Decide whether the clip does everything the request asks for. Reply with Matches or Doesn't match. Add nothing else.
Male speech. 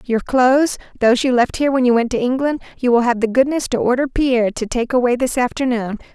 Doesn't match